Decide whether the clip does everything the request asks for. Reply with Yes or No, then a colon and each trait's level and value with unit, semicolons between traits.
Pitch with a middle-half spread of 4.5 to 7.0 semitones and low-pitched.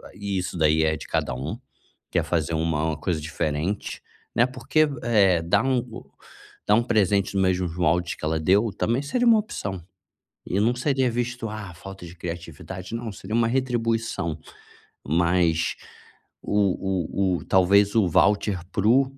Yes: wide, 5.5 semitones; very low, 95 Hz